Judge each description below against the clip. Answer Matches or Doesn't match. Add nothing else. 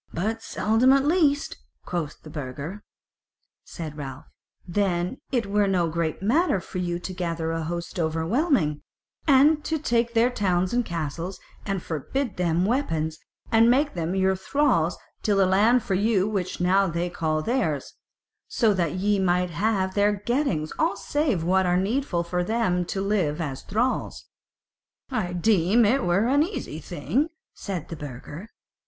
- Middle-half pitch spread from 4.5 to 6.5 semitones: Matches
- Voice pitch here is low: Doesn't match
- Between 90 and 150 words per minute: Doesn't match